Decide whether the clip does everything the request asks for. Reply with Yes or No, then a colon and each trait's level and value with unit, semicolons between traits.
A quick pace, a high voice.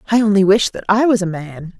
Yes: fast, 270 wpm; high, 200 Hz